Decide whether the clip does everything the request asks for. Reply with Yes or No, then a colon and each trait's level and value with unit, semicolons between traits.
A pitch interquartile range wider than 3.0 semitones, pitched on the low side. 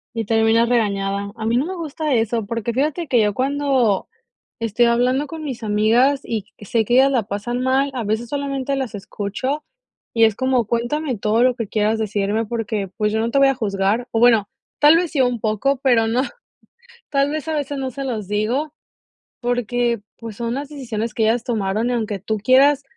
No: average, 3.8 semitones; high, 235 Hz